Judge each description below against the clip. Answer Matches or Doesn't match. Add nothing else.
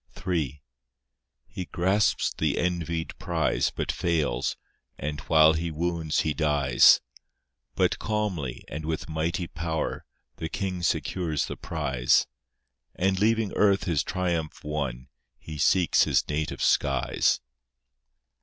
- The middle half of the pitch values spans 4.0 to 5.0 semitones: Doesn't match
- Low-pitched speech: Matches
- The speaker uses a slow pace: Matches